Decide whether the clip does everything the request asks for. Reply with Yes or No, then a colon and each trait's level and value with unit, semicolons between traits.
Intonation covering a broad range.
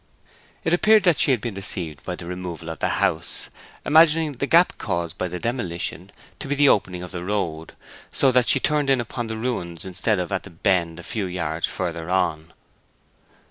Yes: wide, 6.8 semitones